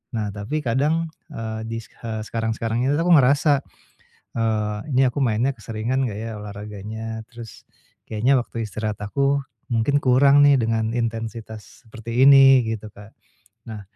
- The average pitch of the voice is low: Yes, low, 115 Hz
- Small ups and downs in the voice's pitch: No, average, 3.4 semitones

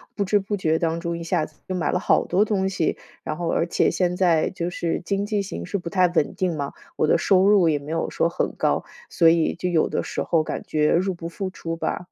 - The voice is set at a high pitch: No, medium, 175 Hz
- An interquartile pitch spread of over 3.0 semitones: No, narrow, 2.5 semitones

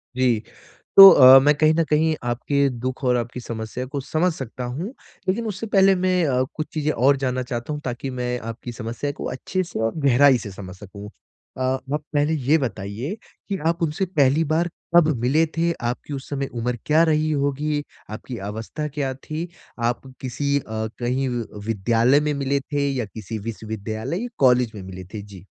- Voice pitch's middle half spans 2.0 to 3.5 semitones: No, average, 4.3 semitones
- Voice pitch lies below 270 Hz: Yes, low, 135 Hz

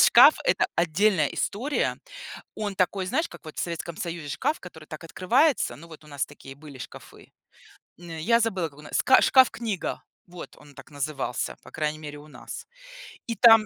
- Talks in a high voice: No, medium, 170 Hz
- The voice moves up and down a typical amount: No, wide, 5.7 semitones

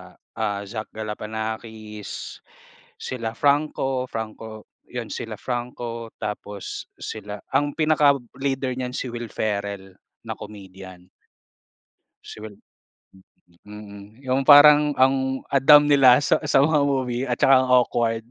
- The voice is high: No, low, 120 Hz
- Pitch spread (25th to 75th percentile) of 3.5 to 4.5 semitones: Yes, average, 4.0 semitones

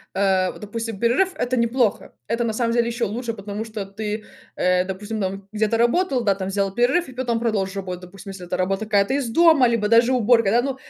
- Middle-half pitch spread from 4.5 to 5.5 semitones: No, average, 3.4 semitones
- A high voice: Yes, high, 220 Hz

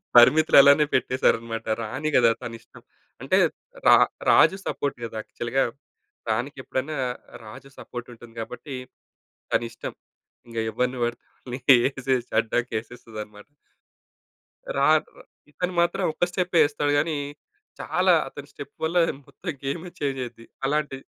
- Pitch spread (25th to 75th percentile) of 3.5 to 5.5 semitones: Yes, average, 4.2 semitones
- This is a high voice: No, low, 130 Hz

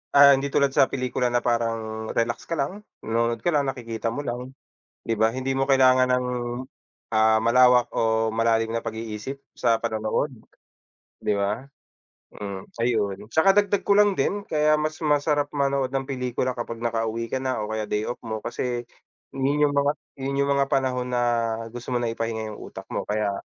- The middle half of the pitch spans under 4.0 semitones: Yes, average, 3.5 semitones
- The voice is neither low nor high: No, low, 125 Hz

